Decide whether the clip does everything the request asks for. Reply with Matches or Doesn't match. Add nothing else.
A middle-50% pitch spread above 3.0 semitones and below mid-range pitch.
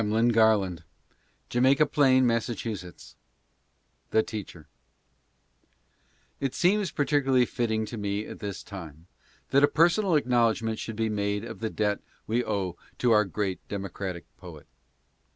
Matches